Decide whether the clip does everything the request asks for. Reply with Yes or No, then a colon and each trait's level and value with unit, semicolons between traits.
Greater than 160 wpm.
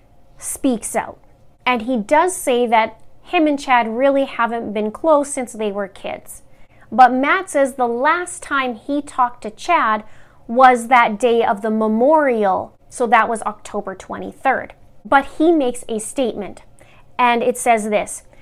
No: average, 155 wpm